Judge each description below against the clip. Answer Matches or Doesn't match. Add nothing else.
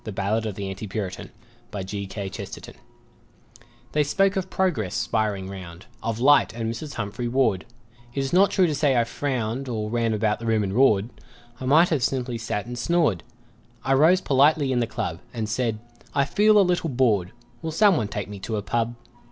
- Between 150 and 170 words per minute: Doesn't match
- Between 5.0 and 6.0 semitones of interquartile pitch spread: Matches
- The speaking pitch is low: Matches